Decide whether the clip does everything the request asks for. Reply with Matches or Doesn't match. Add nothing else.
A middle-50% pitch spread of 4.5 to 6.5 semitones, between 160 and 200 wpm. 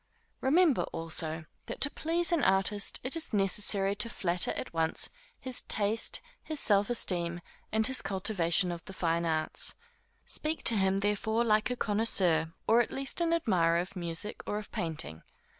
Matches